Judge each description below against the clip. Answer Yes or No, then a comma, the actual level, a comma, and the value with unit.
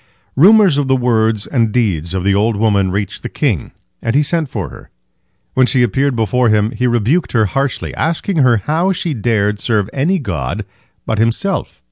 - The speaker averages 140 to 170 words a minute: No, average, 185 wpm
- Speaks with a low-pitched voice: Yes, low, 120 Hz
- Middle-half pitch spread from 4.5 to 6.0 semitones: Yes, average, 5.1 semitones